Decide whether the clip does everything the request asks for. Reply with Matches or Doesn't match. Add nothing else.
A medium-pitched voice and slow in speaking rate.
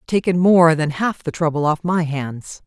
Doesn't match